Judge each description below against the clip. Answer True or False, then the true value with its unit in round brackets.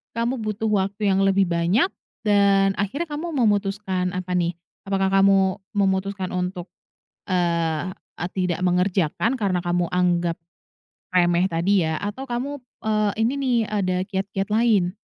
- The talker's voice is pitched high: True (195 Hz)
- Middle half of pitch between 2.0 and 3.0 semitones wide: True (2.6 semitones)